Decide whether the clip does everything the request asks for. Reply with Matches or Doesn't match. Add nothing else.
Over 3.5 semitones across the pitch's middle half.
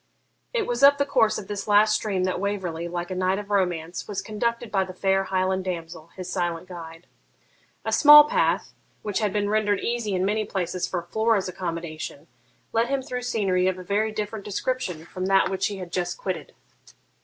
Doesn't match